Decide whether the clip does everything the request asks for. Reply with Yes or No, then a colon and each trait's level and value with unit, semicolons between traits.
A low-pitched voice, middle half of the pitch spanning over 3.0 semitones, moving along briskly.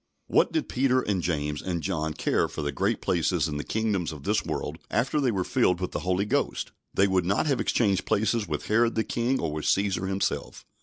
Yes: very low, 95 Hz; average, 5.2 semitones; fast, 220 wpm